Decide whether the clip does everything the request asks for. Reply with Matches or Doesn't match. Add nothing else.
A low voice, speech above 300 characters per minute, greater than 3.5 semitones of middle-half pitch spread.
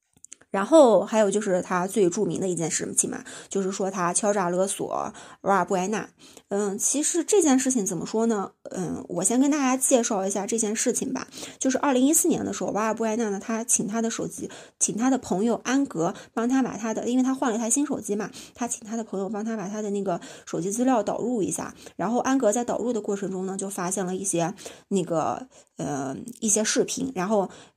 Doesn't match